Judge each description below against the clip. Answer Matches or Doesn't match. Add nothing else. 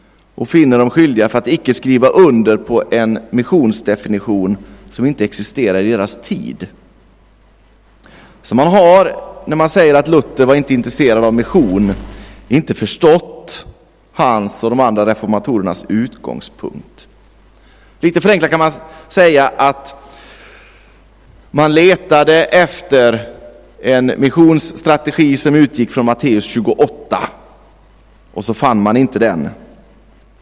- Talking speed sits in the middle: Doesn't match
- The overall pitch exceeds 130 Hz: Doesn't match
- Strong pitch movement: Matches